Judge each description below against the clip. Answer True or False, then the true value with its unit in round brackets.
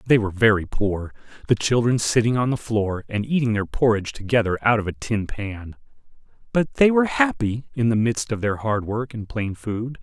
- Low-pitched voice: True (115 Hz)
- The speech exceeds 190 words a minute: True (205 wpm)